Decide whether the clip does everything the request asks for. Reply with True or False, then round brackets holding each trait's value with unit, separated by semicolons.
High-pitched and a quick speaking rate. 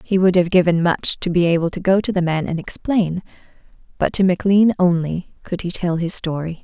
False (180 Hz; 215 wpm)